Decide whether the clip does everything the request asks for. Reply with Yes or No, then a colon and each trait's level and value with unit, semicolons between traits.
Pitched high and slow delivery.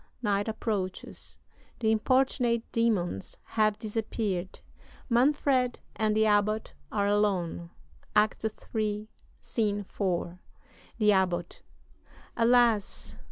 Yes: high, 215 Hz; slow, 90 wpm